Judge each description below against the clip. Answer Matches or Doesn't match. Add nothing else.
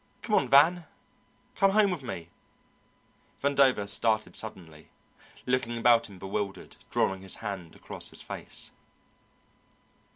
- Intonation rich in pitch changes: Matches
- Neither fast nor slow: Doesn't match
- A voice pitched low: Matches